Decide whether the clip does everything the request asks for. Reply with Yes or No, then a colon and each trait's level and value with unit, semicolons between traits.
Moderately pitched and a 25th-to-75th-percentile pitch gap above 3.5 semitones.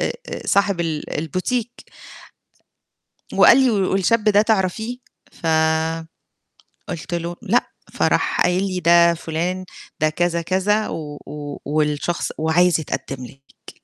Yes: medium, 175 Hz; average, 3.9 semitones